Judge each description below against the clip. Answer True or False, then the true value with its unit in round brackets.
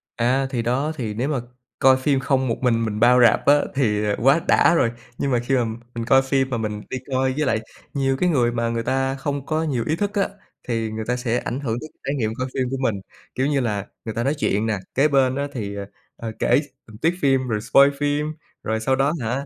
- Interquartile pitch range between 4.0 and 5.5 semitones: False (3.2 semitones)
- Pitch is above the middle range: False (130 Hz)